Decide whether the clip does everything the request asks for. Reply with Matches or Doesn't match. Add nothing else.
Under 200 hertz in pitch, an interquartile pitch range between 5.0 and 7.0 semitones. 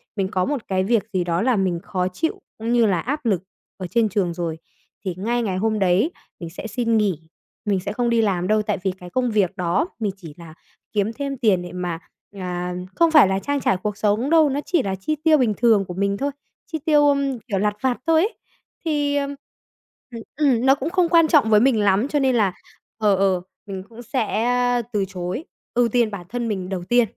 Doesn't match